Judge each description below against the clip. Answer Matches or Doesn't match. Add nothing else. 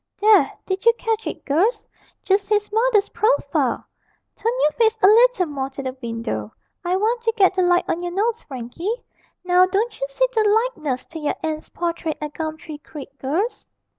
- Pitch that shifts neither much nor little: Doesn't match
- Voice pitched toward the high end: Matches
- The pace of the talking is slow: Doesn't match